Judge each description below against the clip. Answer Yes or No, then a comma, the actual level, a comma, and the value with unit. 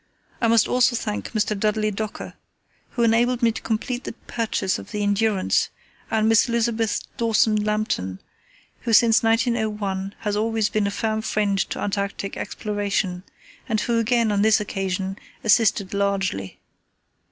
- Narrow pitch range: Yes, narrow, 2.2 semitones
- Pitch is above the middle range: Yes, high, 215 Hz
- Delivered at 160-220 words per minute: No, average, 145 wpm